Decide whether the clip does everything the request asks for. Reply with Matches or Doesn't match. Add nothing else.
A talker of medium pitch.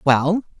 Matches